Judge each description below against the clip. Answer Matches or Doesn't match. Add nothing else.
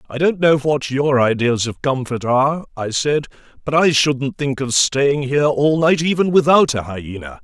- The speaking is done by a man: Matches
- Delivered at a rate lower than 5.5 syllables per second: Matches